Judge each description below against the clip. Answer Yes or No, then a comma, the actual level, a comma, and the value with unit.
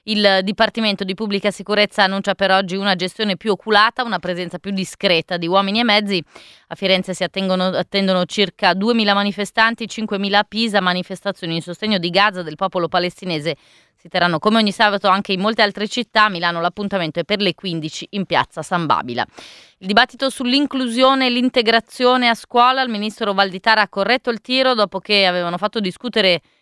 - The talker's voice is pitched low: No, high, 200 Hz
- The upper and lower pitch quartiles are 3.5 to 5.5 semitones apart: No, average, 3.1 semitones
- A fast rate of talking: Yes, fast, 175 wpm